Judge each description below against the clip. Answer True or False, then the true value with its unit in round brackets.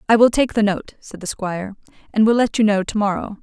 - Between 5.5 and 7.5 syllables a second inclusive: True (6.0 syllables/s)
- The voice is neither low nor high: False (210 Hz)